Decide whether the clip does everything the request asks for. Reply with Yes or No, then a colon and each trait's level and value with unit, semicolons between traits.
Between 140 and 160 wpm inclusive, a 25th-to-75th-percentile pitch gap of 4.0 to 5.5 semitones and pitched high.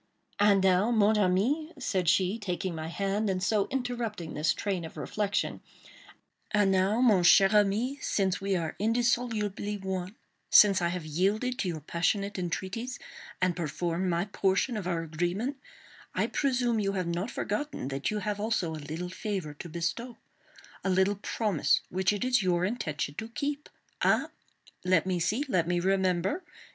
No: average, 155 wpm; average, 3.6 semitones; high, 195 Hz